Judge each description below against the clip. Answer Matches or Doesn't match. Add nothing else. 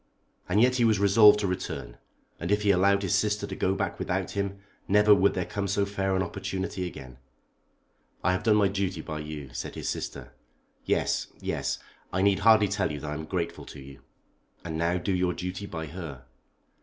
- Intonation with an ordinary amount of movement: Matches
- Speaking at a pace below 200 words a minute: Doesn't match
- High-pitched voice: Doesn't match